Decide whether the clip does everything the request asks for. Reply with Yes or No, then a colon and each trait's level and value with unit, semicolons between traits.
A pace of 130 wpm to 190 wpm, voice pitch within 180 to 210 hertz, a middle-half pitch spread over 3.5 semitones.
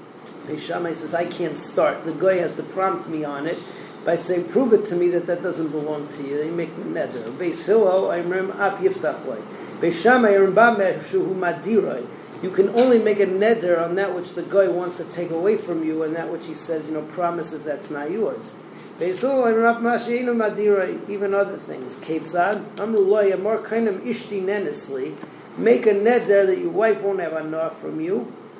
No: fast, 205 wpm; high, 190 Hz; average, 4.1 semitones